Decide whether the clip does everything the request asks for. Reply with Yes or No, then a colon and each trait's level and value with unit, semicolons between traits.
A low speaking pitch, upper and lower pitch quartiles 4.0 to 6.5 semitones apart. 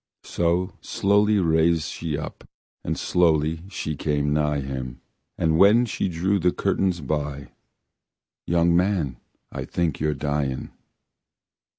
No: very low, 80 Hz; average, 3.5 semitones